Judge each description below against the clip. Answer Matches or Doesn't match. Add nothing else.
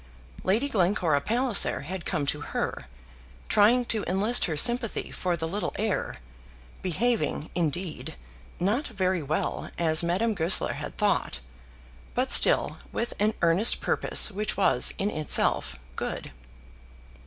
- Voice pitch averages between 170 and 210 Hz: Matches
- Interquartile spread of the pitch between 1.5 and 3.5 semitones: Doesn't match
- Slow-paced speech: Matches